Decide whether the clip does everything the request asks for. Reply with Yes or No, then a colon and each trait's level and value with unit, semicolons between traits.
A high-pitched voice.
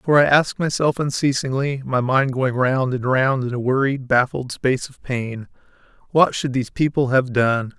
No: low, 130 Hz